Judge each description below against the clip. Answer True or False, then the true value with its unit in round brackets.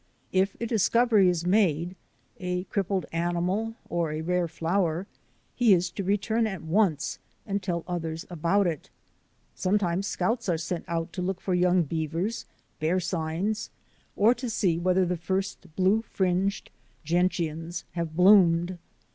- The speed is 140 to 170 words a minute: True (150 wpm)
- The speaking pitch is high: False (180 Hz)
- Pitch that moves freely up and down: False (2.8 semitones)